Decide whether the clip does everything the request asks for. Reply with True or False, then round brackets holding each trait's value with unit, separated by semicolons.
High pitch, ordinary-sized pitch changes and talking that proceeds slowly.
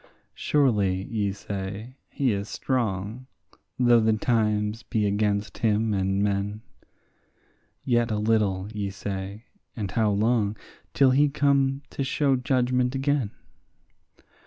False (110 Hz; 3.8 semitones; 120 wpm)